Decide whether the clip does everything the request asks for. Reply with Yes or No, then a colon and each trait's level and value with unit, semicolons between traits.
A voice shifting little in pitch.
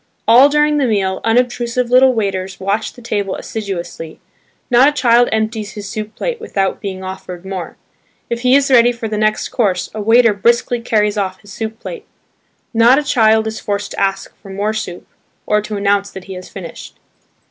No: average, 3.4 semitones